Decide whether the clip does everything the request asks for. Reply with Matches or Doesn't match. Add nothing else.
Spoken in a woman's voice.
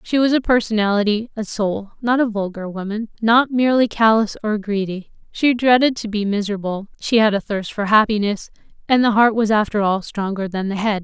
Matches